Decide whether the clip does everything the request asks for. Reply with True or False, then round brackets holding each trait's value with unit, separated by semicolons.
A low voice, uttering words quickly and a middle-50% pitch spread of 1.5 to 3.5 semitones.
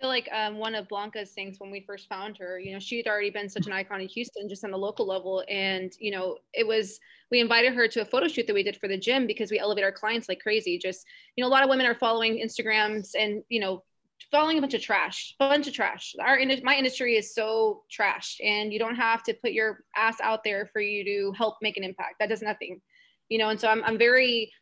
False (220 Hz; 260 wpm; 2.8 semitones)